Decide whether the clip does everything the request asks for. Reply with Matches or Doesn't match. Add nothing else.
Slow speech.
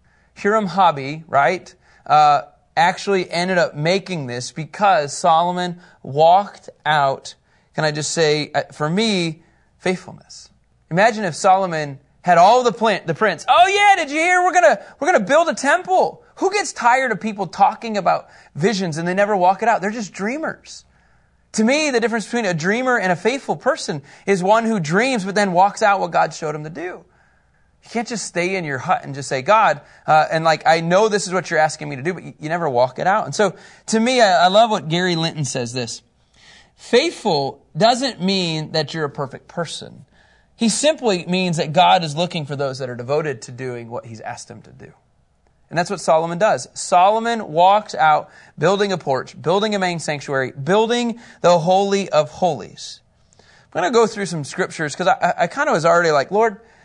Doesn't match